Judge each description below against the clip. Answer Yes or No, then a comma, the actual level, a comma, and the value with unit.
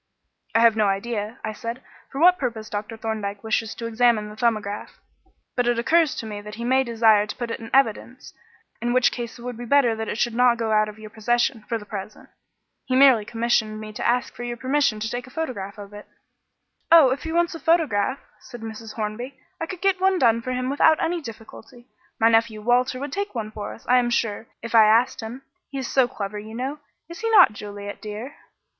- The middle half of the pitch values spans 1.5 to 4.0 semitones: Yes, average, 3.1 semitones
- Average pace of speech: No, fast, 225 wpm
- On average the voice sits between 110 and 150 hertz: No, high, 235 Hz